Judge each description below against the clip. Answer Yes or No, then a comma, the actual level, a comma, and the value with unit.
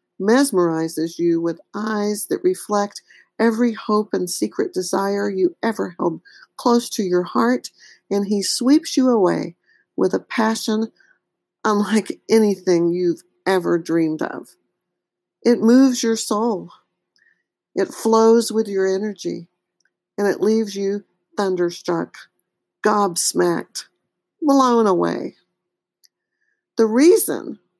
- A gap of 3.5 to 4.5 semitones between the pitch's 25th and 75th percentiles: Yes, average, 3.8 semitones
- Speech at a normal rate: No, slow, 110 wpm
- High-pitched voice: Yes, high, 210 Hz